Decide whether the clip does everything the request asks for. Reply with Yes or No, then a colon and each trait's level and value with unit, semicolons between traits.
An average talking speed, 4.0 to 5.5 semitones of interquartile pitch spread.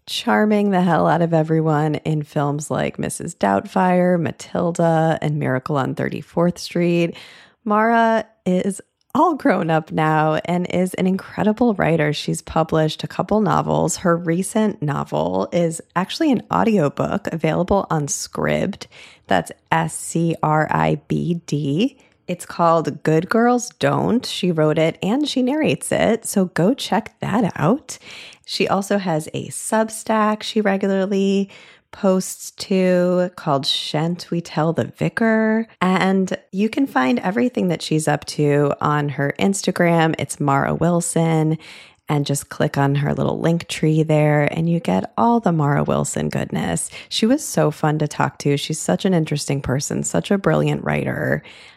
Yes: average, 150 wpm; average, 4.7 semitones